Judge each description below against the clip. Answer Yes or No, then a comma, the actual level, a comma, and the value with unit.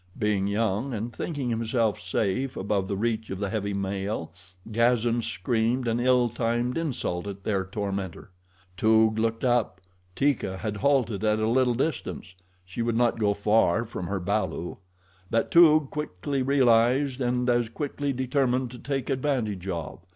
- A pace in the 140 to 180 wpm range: Yes, average, 155 wpm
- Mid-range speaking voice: No, low, 115 Hz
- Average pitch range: Yes, average, 3.8 semitones